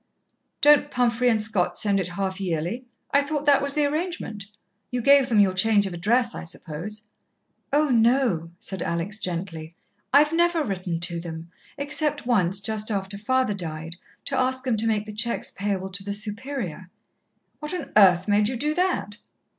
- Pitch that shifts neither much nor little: No, wide, 6.0 semitones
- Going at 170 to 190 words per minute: Yes, average, 180 wpm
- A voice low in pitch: No, high, 215 Hz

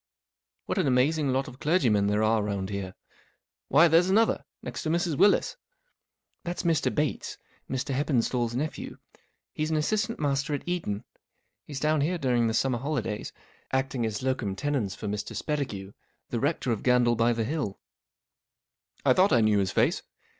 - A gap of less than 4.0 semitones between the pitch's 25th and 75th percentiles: No, wide, 5.5 semitones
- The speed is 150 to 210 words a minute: Yes, average, 175 wpm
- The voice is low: Yes, low, 130 Hz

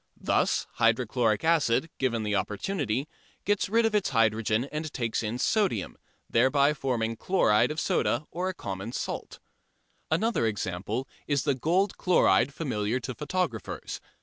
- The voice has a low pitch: Yes, low, 130 Hz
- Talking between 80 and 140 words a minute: Yes, slow, 135 wpm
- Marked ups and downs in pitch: Yes, wide, 6.3 semitones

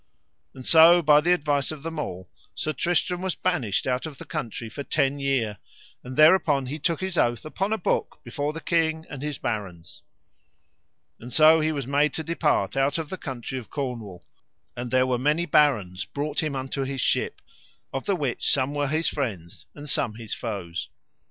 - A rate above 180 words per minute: Yes, average, 190 wpm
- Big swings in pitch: No, average, 4.2 semitones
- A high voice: No, medium, 140 Hz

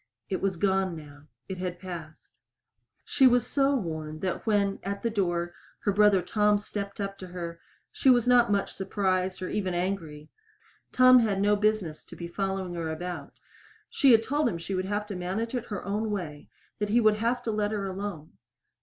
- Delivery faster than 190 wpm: Yes, average, 200 wpm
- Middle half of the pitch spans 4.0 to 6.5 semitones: No, average, 3.2 semitones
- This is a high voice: Yes, high, 195 Hz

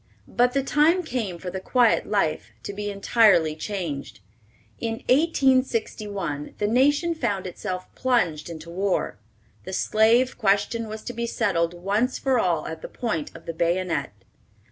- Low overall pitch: No, high, 205 Hz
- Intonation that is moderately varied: No, wide, 6.0 semitones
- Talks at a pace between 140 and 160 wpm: Yes, average, 150 wpm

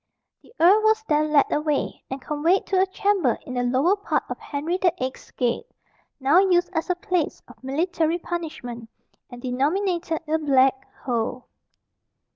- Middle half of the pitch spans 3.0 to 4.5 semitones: No, average, 5.3 semitones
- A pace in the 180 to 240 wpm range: No, average, 160 wpm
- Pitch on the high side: Yes, very high, 315 Hz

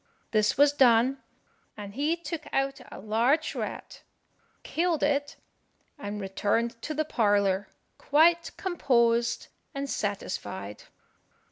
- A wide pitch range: Yes, wide, 5.8 semitones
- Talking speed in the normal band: No, slow, 110 wpm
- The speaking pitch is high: Yes, high, 245 Hz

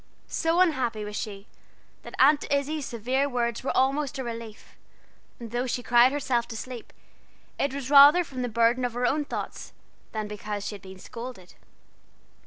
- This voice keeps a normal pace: Yes, average, 175 wpm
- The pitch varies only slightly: No, average, 3.4 semitones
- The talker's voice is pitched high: Yes, high, 245 Hz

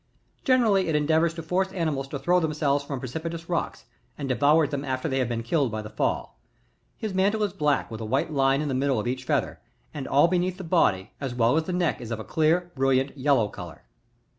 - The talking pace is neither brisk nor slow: No, fast, 225 wpm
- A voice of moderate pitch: Yes, medium, 145 Hz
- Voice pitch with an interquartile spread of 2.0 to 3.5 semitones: No, average, 4.5 semitones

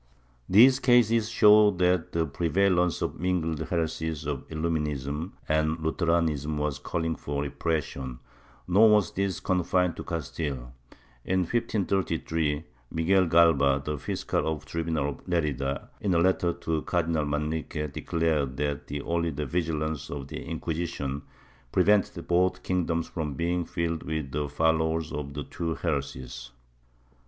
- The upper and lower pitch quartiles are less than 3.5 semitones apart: Yes, average, 3.1 semitones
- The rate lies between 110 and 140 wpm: Yes, slow, 135 wpm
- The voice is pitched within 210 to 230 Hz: No, very low, 80 Hz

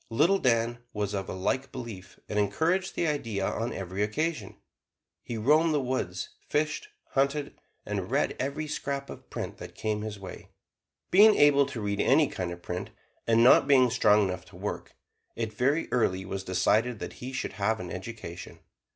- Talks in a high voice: No, low, 115 Hz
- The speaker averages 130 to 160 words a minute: No, average, 175 wpm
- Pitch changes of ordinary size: No, wide, 6.0 semitones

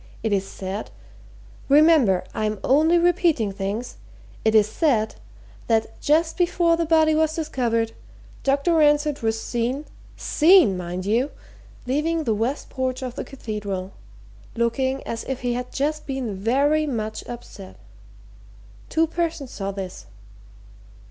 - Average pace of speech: No, slow, 125 wpm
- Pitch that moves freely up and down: Yes, wide, 6.1 semitones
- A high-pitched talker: Yes, very high, 255 Hz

